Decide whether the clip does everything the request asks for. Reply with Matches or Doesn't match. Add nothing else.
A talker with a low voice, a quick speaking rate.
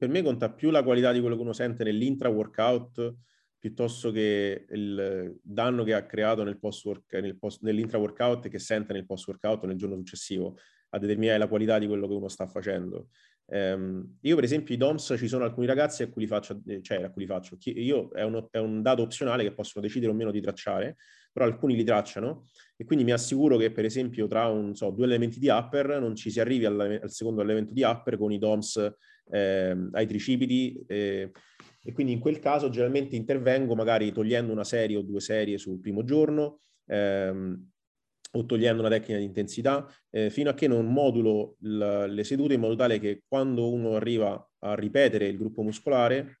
Matches